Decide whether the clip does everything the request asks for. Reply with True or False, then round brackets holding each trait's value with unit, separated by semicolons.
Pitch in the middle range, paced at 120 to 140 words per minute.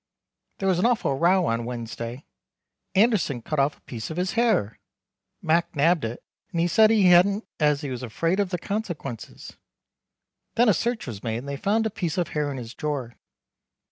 False (165 Hz; 195 wpm)